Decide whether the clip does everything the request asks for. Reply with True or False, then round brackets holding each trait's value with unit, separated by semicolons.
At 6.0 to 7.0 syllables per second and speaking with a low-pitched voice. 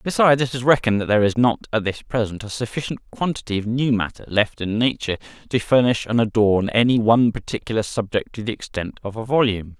True (6.3 syllables/s; 115 Hz)